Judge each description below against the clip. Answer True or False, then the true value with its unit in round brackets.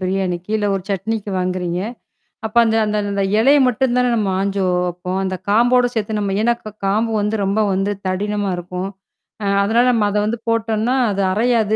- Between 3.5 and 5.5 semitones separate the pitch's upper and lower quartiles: False (2.9 semitones)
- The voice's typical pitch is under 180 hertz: False (205 Hz)